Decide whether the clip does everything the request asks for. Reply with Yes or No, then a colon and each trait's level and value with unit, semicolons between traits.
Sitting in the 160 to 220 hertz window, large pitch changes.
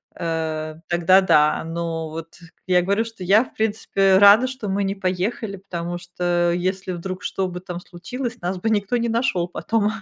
No: medium, 185 Hz; average, 2.9 semitones